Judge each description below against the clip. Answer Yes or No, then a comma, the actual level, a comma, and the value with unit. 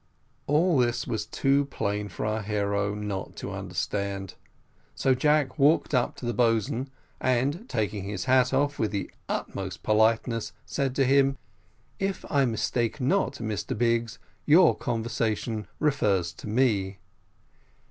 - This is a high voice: No, low, 115 Hz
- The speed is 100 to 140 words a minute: Yes, slow, 135 wpm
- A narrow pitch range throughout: No, average, 4.6 semitones